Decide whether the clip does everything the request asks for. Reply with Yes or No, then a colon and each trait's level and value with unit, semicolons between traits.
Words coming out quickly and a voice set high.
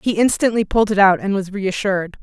Yes: fast, 215 wpm; high, 200 Hz